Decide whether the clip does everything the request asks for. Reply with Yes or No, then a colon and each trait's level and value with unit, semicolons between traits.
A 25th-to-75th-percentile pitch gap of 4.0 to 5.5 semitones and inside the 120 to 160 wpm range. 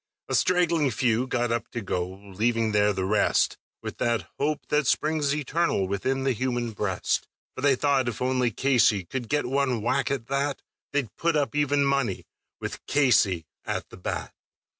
No: average, 4.3 semitones; average, 175 wpm